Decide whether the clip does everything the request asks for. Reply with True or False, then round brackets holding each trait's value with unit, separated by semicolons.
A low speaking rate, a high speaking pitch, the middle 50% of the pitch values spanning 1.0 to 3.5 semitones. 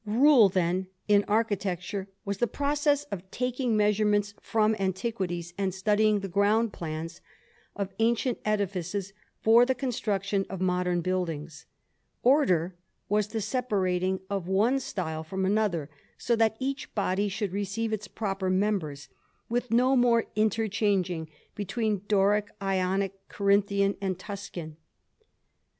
True (125 wpm; 200 Hz; 2.9 semitones)